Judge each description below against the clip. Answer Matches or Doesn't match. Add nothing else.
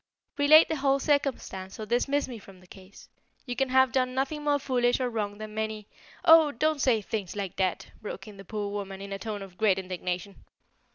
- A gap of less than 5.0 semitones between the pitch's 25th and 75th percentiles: Doesn't match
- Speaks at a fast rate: Matches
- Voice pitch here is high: Matches